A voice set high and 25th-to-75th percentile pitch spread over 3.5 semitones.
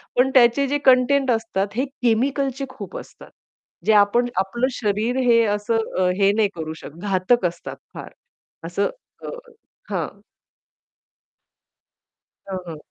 Yes: high, 230 Hz; average, 4.5 semitones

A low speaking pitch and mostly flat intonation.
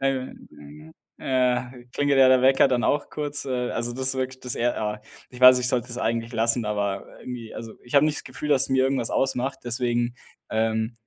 Yes: low, 125 Hz; narrow, 2.0 semitones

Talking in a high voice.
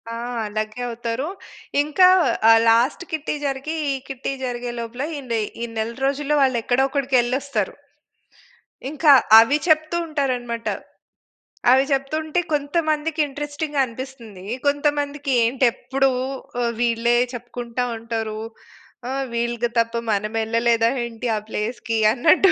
Yes: very high, 255 Hz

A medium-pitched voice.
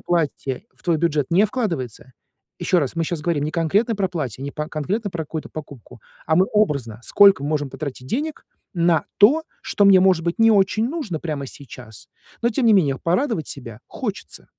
Yes: medium, 165 Hz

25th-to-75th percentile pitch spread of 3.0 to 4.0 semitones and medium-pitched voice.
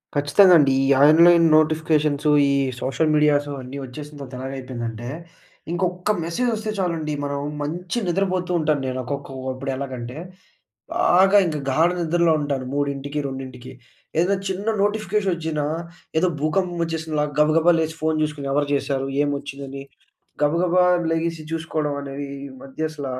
Yes: average, 3.6 semitones; medium, 150 Hz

